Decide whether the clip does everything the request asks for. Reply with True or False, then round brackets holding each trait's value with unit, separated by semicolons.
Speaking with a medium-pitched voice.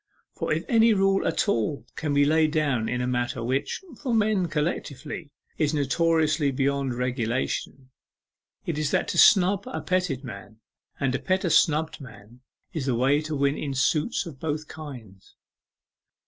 True (145 Hz)